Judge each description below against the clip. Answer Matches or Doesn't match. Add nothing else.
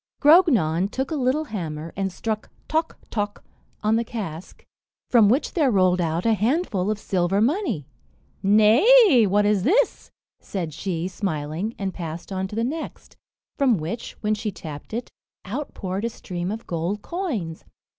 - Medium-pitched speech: Doesn't match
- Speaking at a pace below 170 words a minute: Matches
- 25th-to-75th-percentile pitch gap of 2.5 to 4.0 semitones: Doesn't match